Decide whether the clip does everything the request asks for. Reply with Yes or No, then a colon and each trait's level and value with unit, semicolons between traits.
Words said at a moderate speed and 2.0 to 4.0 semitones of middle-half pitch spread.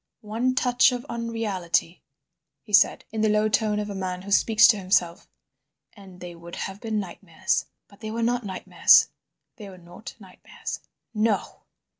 Yes: average, 160 wpm; average, 3.2 semitones